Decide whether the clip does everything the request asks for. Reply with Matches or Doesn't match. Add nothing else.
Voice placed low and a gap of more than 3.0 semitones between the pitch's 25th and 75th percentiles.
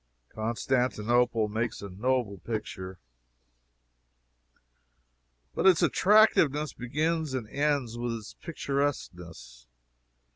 Matches